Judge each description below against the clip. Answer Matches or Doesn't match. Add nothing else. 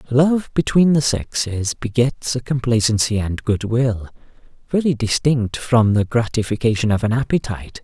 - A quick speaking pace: Doesn't match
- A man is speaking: Matches